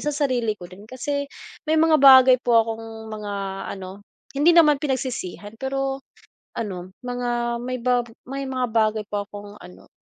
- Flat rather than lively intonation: No, average, 4.2 semitones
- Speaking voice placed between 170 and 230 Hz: No, high, 245 Hz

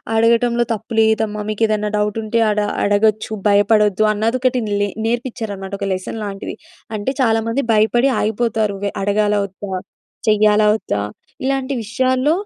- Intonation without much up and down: Yes, narrow, 2.1 semitones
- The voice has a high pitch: Yes, high, 215 Hz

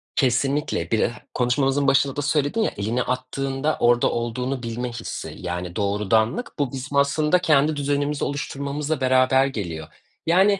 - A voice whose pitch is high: No, low, 135 Hz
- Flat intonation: No, average, 3.1 semitones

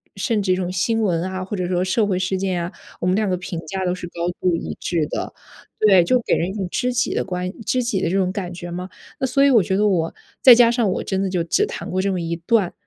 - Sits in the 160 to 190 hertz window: Yes, medium, 185 Hz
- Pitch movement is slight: No, average, 3.0 semitones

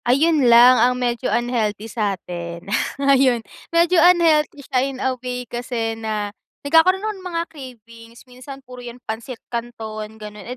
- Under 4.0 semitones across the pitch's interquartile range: Yes, average, 3.5 semitones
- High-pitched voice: Yes, high, 245 Hz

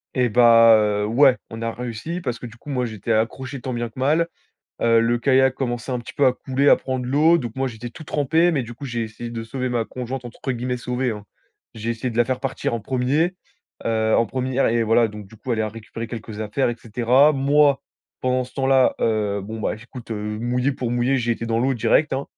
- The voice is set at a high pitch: No, low, 120 Hz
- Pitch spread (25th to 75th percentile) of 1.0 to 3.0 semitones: Yes, narrow, 2.6 semitones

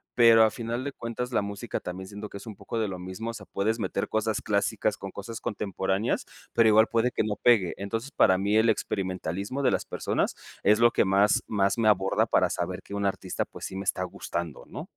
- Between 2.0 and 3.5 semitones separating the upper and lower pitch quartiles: Yes, narrow, 2.6 semitones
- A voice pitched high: No, low, 105 Hz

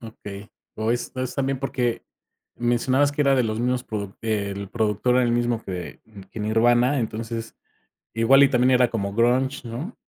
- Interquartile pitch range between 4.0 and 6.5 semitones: No, average, 2.7 semitones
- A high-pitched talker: No, low, 120 Hz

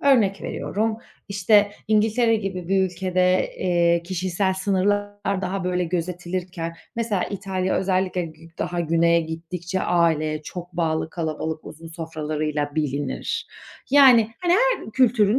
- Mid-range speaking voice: Yes, medium, 180 Hz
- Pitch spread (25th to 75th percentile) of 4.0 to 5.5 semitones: No, average, 3.5 semitones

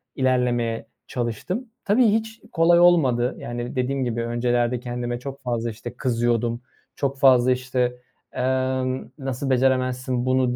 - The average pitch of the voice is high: No, low, 125 Hz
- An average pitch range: No, narrow, 1.7 semitones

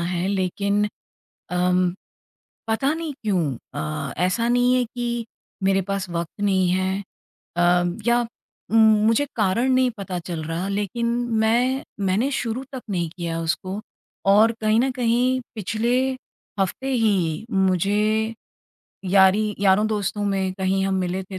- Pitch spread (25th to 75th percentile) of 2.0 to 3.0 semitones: No, average, 3.8 semitones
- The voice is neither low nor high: No, high, 200 Hz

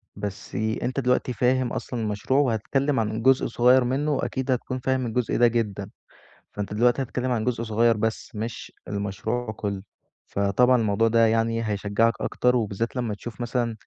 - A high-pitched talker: No, low, 115 Hz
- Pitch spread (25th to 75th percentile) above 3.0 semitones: No, narrow, 2.6 semitones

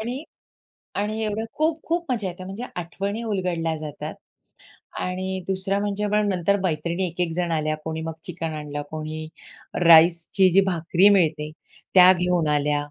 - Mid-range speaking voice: Yes, medium, 180 Hz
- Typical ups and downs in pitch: Yes, average, 3.7 semitones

